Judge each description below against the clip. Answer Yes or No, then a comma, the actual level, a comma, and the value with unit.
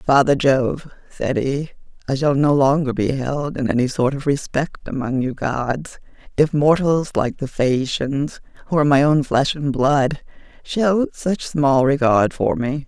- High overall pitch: No, medium, 140 Hz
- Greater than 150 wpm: Yes, average, 170 wpm